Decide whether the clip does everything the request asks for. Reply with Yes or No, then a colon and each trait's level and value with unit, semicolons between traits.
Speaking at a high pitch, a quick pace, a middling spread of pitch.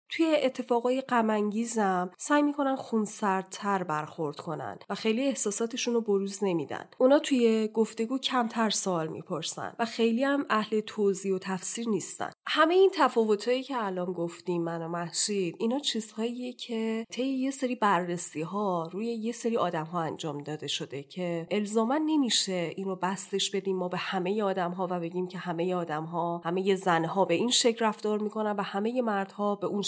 Yes: high, 205 Hz; fast, 165 wpm; average, 4.6 semitones